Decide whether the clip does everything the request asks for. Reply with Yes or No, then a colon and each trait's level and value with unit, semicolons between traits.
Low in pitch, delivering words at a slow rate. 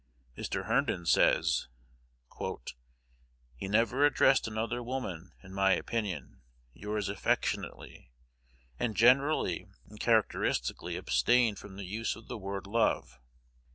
Yes: low, 105 Hz; slow, 110 wpm